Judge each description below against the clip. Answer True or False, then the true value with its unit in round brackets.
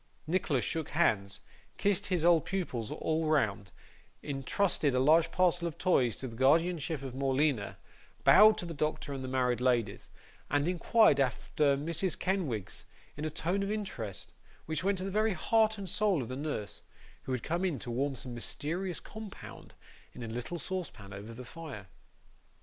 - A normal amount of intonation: False (6.1 semitones)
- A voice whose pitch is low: False (155 Hz)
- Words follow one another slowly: False (170 wpm)